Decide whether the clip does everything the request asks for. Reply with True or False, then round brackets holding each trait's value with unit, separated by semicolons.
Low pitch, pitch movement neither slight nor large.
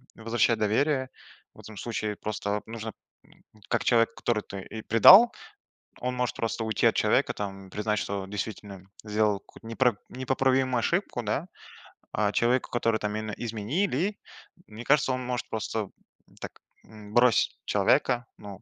True (115 Hz; 3.0 semitones)